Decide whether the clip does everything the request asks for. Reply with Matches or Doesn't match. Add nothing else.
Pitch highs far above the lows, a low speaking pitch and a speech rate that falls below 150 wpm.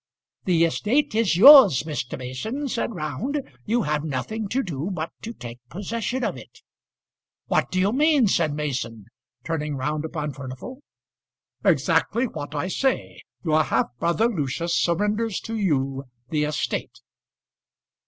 Doesn't match